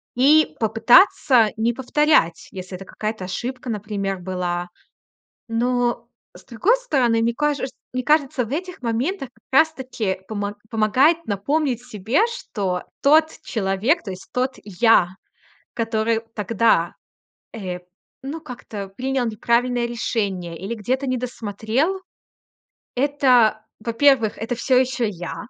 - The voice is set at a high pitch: Yes, high, 235 Hz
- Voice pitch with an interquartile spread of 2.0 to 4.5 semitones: Yes, average, 4.2 semitones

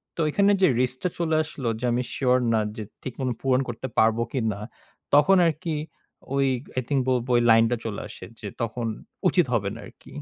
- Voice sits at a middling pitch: No, low, 125 Hz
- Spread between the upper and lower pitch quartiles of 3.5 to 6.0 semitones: Yes, average, 3.9 semitones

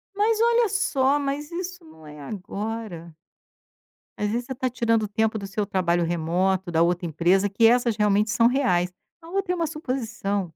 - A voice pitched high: Yes, high, 220 Hz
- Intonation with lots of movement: Yes, wide, 6.9 semitones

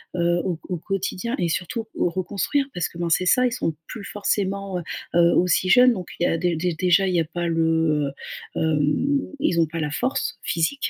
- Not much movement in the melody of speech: No, average, 3.2 semitones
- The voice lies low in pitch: No, medium, 175 Hz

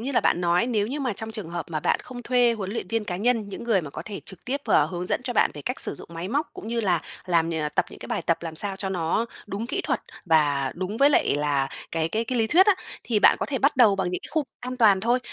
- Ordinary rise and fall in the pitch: No, wide, 5.8 semitones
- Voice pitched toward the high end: Yes, high, 205 Hz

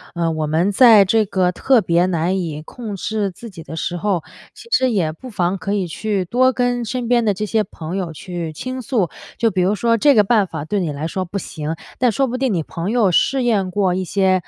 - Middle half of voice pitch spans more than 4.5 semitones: Yes, average, 4.9 semitones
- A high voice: Yes, high, 195 Hz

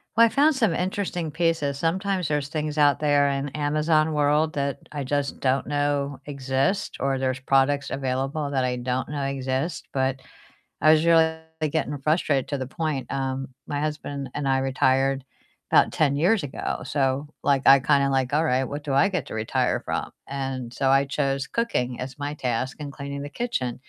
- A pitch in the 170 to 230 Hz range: No, medium, 140 Hz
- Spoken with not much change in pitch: Yes, narrow, 2.3 semitones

